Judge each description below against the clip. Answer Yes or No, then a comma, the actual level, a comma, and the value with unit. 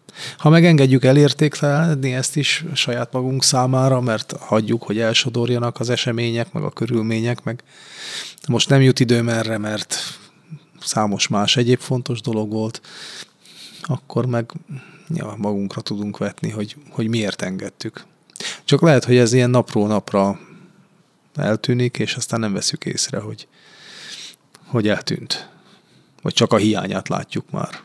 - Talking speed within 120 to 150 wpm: Yes, average, 135 wpm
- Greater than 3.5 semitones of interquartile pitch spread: Yes, average, 4.1 semitones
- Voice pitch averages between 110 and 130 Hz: Yes, low, 120 Hz